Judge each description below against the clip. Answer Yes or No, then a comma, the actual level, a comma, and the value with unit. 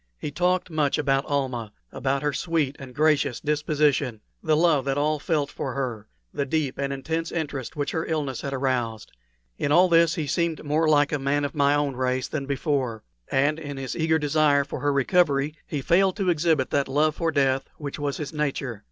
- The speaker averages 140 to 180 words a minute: No, average, 200 wpm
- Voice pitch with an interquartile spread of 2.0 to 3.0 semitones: Yes, narrow, 2.4 semitones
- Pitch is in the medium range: Yes, medium, 145 Hz